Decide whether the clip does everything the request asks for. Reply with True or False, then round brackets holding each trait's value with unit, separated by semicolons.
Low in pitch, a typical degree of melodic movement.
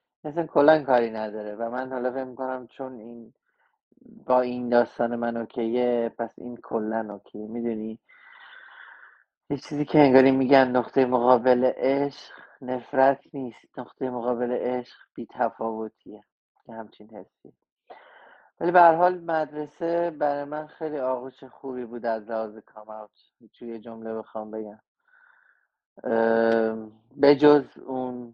True (125 Hz; 4.0 semitones)